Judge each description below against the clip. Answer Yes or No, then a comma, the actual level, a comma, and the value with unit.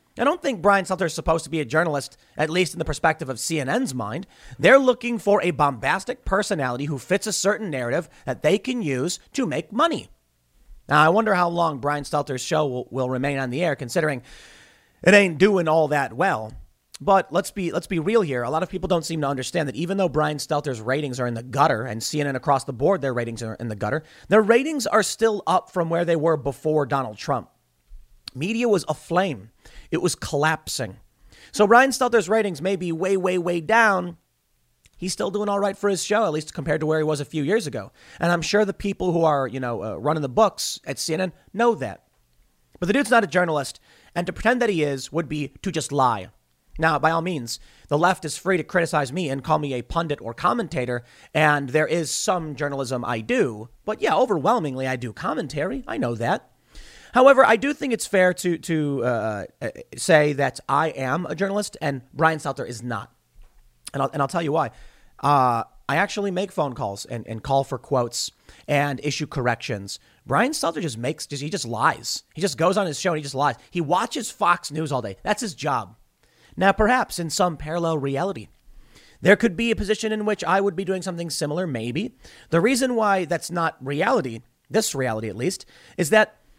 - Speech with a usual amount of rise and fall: No, wide, 5.8 semitones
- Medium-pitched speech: Yes, medium, 160 Hz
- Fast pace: Yes, fast, 215 wpm